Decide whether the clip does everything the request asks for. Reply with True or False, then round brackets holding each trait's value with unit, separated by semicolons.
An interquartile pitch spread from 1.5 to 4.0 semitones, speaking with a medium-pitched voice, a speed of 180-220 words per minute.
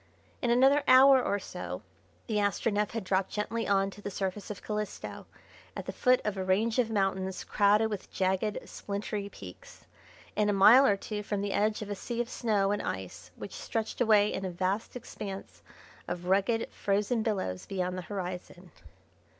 False (2.4 semitones; 205 Hz; 185 wpm)